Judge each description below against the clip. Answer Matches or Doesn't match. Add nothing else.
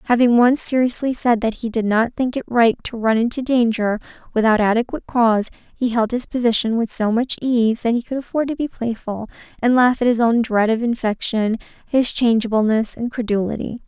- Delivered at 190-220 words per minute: Matches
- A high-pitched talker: Matches